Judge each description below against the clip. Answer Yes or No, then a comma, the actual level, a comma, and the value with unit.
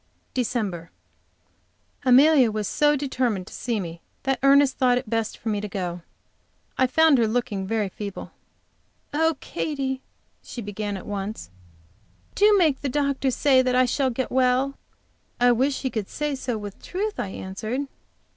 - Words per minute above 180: No, average, 160 wpm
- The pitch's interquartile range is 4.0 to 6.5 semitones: Yes, average, 4.6 semitones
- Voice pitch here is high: Yes, very high, 250 Hz